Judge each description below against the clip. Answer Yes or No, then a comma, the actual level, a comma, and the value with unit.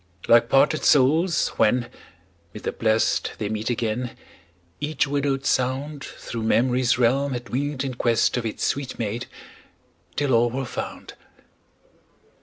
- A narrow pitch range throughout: No, average, 3.1 semitones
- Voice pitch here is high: No, low, 125 Hz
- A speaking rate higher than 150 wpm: No, slow, 135 wpm